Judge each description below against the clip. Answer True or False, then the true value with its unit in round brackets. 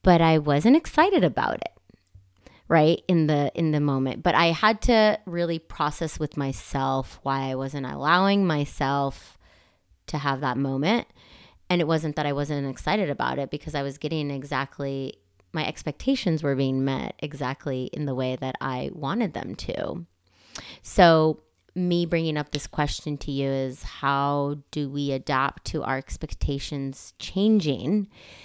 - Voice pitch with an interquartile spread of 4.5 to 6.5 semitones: False (3.5 semitones)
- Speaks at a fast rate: False (155 wpm)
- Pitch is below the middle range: False (145 Hz)